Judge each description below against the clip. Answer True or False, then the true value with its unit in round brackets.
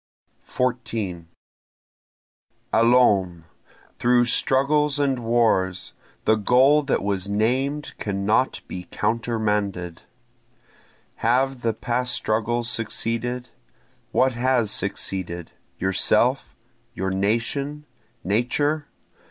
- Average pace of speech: False (80 wpm)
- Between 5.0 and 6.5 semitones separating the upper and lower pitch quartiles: False (4.1 semitones)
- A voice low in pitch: True (115 Hz)